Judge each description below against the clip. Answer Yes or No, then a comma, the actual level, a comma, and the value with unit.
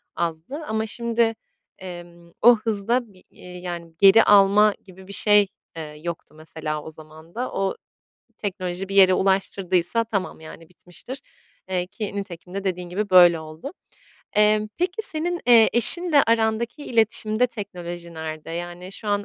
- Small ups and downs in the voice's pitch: No, average, 4.2 semitones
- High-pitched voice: Yes, high, 195 Hz